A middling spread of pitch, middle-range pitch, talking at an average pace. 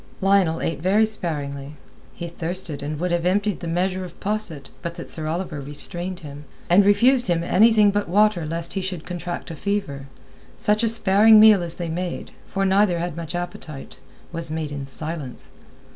Yes: average, 3.7 semitones; medium, 175 Hz; average, 175 wpm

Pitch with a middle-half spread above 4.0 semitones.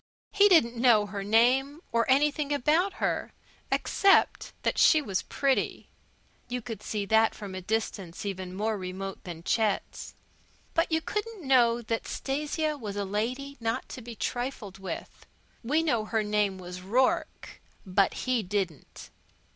Yes: wide, 5.5 semitones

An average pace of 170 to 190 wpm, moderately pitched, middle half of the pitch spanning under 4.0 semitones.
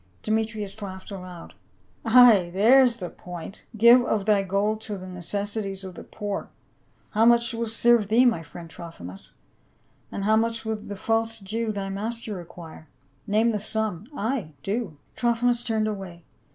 No: average, 175 wpm; high, 210 Hz; average, 3.1 semitones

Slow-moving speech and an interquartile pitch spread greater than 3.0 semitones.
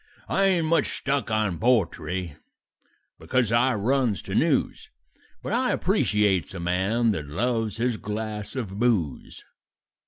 Yes: slow, 130 wpm; average, 4.5 semitones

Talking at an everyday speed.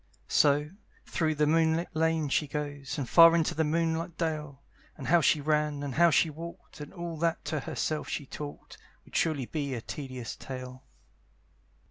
Yes: average, 170 wpm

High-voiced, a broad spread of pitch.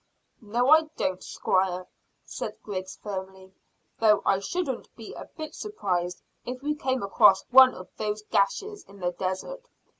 Yes: high, 210 Hz; wide, 5.8 semitones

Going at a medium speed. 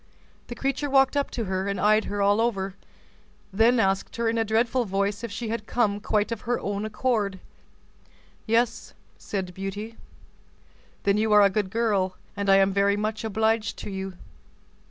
Yes: average, 175 wpm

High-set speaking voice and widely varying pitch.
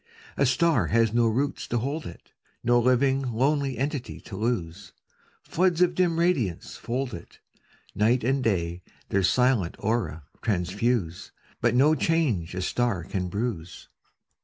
No: low, 120 Hz; wide, 6.1 semitones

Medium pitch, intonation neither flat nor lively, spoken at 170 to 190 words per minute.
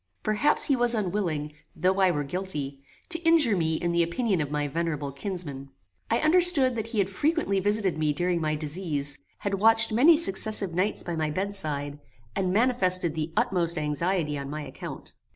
No: medium, 180 Hz; wide, 5.8 semitones; average, 175 wpm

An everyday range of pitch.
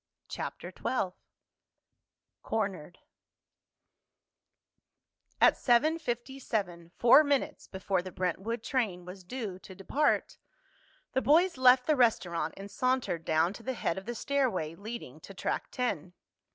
No: wide, 6.1 semitones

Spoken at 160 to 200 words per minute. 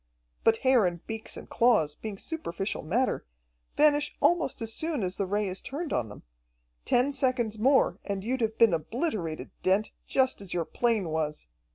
Yes: average, 175 wpm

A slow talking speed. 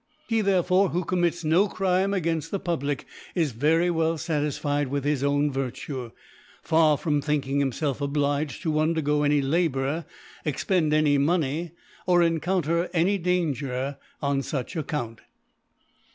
No: average, 145 wpm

